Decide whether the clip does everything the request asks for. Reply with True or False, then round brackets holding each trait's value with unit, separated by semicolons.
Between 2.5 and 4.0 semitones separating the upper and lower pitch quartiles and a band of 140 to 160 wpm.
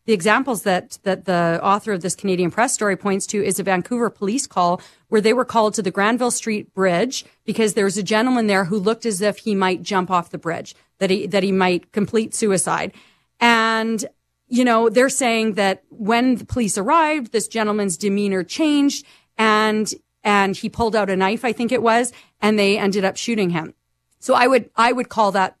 False (3.1 semitones; 205 wpm)